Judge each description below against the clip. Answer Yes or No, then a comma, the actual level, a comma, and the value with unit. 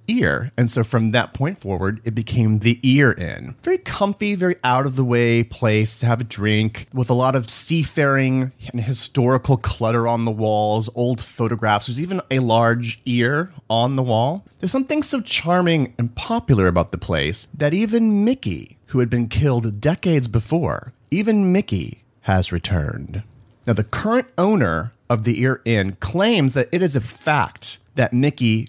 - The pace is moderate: Yes, average, 175 wpm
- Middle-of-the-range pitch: No, low, 120 Hz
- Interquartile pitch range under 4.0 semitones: No, average, 4.6 semitones